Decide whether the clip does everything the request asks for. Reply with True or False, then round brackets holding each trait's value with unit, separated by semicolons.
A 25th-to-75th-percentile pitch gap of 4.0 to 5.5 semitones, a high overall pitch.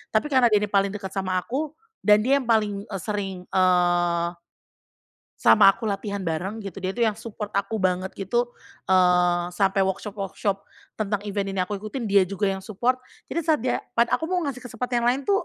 False (3.6 semitones; 205 Hz)